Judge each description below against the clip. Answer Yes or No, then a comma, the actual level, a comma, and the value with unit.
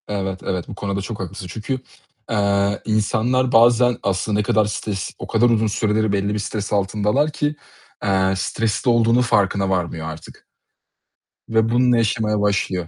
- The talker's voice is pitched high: No, low, 105 Hz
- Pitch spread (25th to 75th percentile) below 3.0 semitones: Yes, narrow, 2.6 semitones